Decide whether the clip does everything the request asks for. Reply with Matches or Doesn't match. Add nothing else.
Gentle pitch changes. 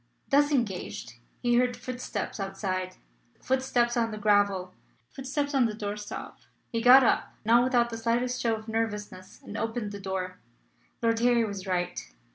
Doesn't match